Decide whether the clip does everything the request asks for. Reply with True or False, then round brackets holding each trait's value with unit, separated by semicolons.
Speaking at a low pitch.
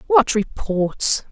False (235 Hz)